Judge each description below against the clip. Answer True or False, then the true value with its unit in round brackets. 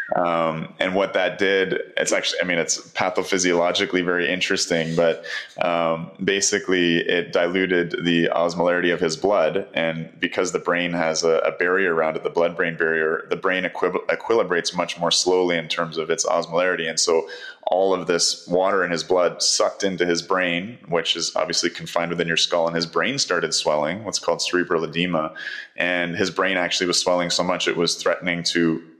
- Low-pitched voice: True (85 Hz)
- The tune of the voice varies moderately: False (1.5 semitones)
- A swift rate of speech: False (185 wpm)